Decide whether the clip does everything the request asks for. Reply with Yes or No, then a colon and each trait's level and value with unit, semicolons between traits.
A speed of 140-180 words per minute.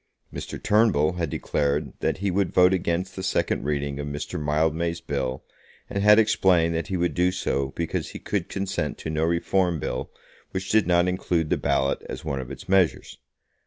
No: average, 190 wpm